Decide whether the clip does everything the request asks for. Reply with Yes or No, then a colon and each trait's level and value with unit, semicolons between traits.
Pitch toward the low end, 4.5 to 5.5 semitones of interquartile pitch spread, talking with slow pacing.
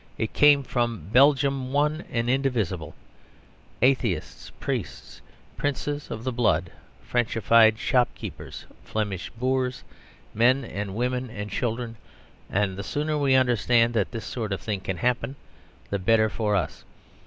No: low, 120 Hz; average, 3.8 semitones; slow, 130 wpm